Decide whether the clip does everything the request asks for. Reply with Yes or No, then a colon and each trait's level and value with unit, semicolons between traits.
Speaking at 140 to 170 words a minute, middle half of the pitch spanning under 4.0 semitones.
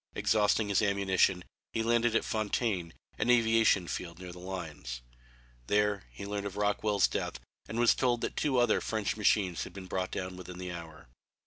No: average, 180 wpm; average, 3.3 semitones